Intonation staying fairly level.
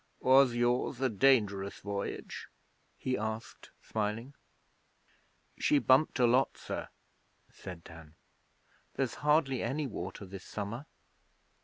No: average, 4.6 semitones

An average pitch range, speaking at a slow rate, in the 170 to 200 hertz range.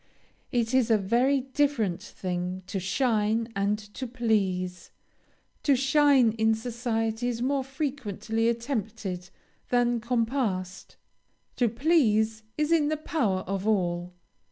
No: average, 4.5 semitones; slow, 120 wpm; high, 225 Hz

